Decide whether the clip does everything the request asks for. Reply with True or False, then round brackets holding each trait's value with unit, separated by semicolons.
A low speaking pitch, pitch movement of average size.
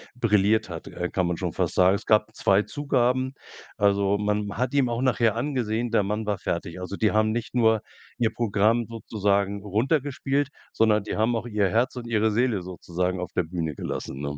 True (110 Hz; 3.3 semitones)